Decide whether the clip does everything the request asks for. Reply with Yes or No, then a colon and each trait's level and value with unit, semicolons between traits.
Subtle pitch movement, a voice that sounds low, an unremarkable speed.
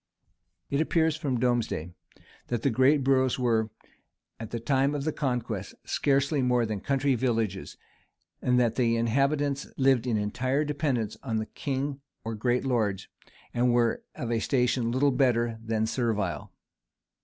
No: average, 3.2 semitones; low, 125 Hz; average, 150 wpm